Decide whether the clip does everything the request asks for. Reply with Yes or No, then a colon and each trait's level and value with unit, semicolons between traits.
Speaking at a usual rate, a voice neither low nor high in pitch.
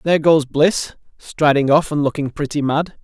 Yes: average, 180 wpm; medium, 150 Hz